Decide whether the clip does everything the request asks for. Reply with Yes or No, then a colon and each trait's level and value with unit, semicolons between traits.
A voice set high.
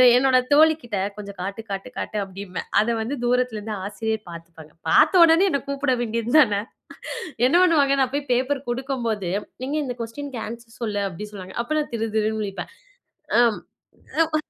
Yes: high, 230 Hz